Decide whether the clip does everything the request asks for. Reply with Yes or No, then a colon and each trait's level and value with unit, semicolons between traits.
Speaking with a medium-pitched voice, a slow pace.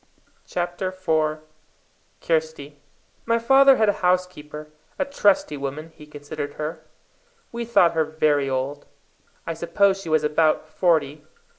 Yes: medium, 160 Hz; slow, 130 wpm